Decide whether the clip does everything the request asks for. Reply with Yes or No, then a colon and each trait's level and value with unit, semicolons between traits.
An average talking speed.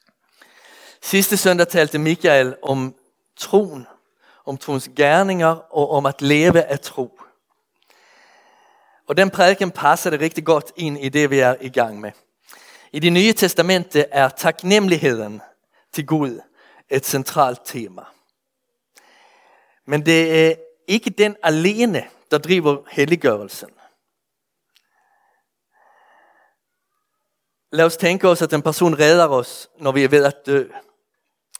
No: slow, 125 wpm